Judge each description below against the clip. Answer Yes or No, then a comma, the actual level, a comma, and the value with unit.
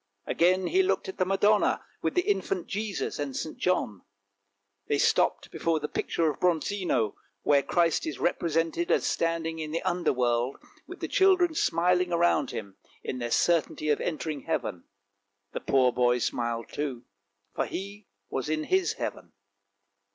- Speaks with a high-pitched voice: No, medium, 165 Hz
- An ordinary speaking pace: Yes, average, 160 wpm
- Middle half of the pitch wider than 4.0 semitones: Yes, average, 5.3 semitones